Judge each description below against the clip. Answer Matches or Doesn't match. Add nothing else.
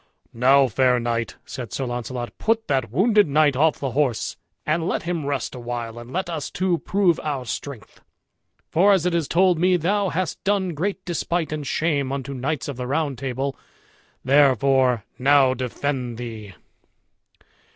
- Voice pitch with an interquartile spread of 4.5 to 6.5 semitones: Matches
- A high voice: Doesn't match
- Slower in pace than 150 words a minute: Doesn't match